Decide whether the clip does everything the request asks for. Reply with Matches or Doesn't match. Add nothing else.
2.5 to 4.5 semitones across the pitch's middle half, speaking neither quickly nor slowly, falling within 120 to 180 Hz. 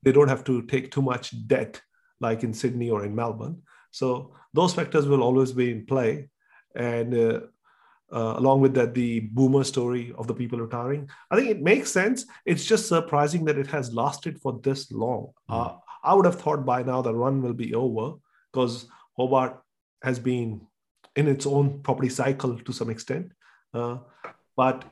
Matches